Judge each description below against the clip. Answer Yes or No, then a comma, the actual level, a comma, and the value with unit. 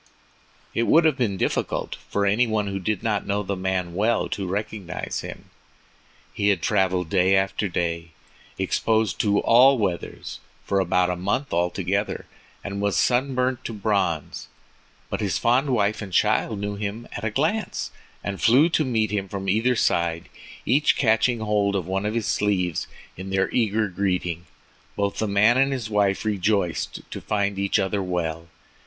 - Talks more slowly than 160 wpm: No, average, 170 wpm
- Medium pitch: No, low, 100 Hz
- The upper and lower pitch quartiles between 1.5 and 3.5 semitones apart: Yes, average, 2.8 semitones